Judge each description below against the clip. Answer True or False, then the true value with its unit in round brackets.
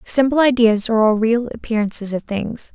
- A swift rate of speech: False (175 wpm)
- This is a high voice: True (230 Hz)